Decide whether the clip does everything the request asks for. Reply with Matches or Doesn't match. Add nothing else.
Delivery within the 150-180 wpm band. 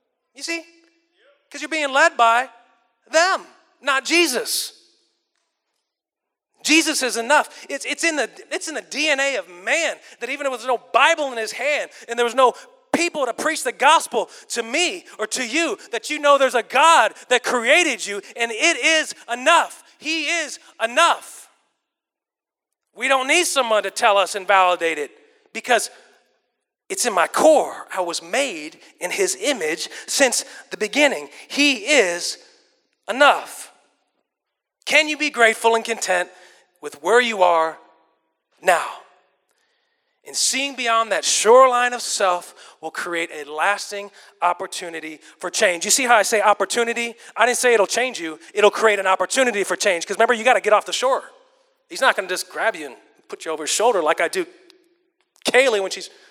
Matches